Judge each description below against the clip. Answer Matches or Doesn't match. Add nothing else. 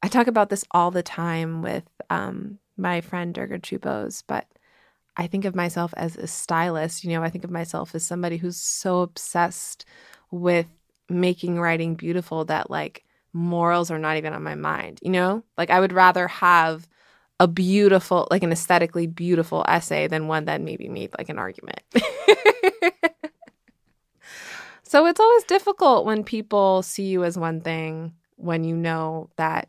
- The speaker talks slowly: Doesn't match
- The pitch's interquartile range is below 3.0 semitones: Matches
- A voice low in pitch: Doesn't match